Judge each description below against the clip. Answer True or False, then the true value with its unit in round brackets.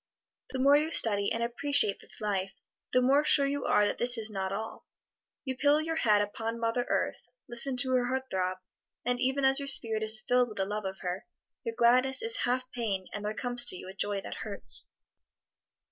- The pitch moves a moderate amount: True (4.1 semitones)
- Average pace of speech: False (210 wpm)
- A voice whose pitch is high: True (240 Hz)